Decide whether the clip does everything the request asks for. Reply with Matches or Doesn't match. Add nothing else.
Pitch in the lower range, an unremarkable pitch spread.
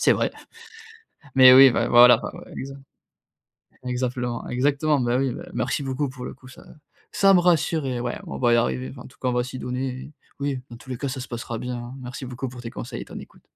Doesn't match